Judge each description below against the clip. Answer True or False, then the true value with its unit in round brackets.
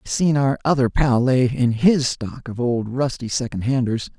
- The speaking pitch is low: True (125 Hz)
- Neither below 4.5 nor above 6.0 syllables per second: True (4.6 syllables/s)